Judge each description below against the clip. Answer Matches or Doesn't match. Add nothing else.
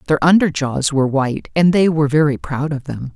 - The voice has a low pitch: Doesn't match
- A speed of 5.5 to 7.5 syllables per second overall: Matches